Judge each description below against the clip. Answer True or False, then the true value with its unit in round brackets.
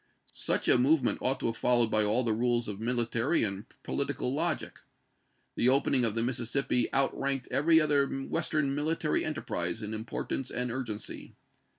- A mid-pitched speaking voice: False (125 Hz)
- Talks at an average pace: True (165 wpm)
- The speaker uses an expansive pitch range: False (3.4 semitones)